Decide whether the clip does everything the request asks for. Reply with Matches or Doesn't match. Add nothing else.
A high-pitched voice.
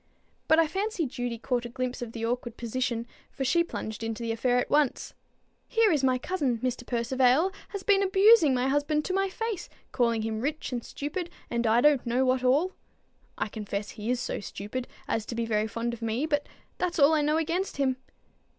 Matches